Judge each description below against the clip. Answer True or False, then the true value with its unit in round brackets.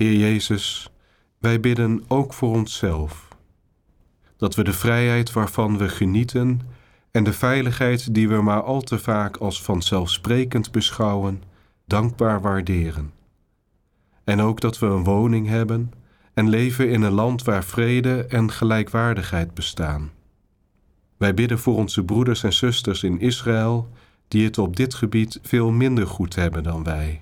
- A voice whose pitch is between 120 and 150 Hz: False (110 Hz)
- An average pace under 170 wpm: True (145 wpm)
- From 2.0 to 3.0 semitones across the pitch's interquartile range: False (3.5 semitones)